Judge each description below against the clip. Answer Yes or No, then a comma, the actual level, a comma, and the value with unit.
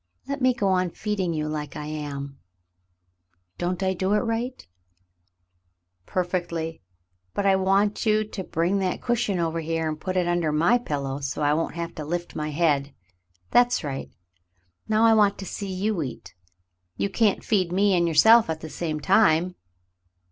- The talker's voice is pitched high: No, medium, 175 Hz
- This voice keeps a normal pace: Yes, average, 175 wpm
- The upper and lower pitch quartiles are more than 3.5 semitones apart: Yes, average, 4.7 semitones